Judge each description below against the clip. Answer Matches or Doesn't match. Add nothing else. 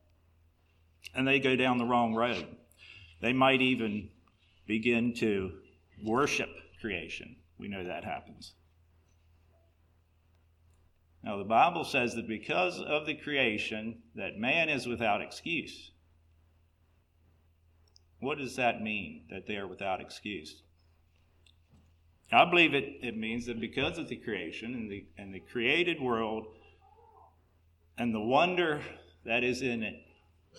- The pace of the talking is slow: Matches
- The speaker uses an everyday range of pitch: Doesn't match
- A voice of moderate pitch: Doesn't match